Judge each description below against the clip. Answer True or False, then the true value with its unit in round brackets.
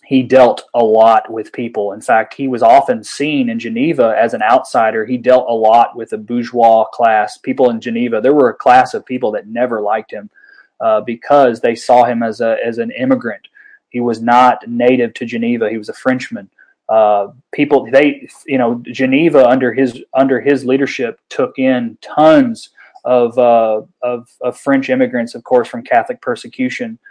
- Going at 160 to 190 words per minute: True (185 wpm)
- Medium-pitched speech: False (130 Hz)